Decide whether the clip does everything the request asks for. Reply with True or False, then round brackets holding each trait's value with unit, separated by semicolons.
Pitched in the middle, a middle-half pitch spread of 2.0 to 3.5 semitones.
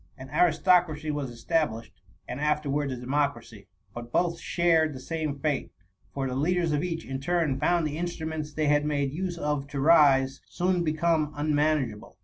True (150 Hz; 3.1 semitones)